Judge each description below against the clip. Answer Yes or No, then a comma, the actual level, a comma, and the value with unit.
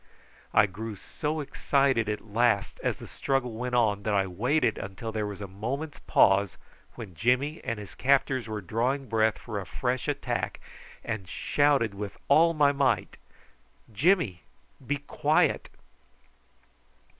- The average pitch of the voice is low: Yes, low, 115 Hz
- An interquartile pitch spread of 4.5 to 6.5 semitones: Yes, average, 5.1 semitones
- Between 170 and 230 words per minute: No, average, 145 wpm